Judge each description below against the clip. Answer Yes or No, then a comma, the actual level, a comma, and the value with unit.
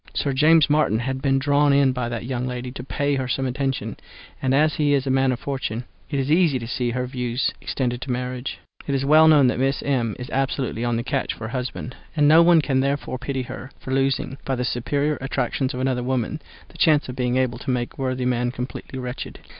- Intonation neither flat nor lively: No, narrow, 2.0 semitones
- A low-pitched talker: Yes, low, 130 Hz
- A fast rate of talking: Yes, fast, 235 wpm